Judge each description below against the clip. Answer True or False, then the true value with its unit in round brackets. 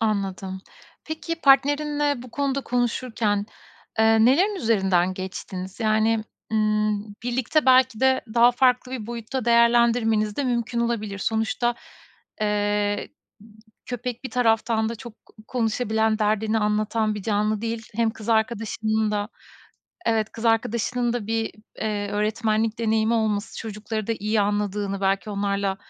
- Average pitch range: False (2.2 semitones)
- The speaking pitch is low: False (220 Hz)